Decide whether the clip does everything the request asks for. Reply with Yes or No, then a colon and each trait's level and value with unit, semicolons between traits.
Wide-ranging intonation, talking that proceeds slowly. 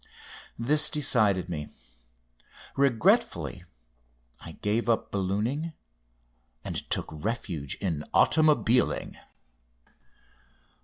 Yes: wide, 6.7 semitones; slow, 70 wpm